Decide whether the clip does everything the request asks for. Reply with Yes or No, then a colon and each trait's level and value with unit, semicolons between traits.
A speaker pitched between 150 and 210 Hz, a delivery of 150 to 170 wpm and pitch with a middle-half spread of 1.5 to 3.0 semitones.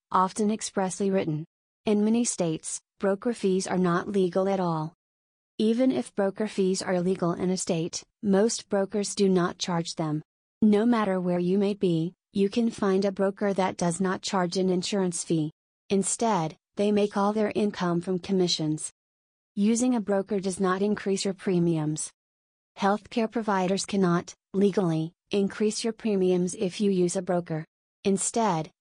Yes: high, 190 Hz; average, 155 wpm; narrow, 2.5 semitones